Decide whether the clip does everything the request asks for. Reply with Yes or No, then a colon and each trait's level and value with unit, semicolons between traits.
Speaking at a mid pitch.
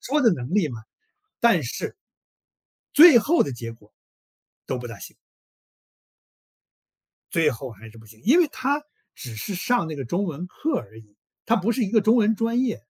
Yes: medium, 180 Hz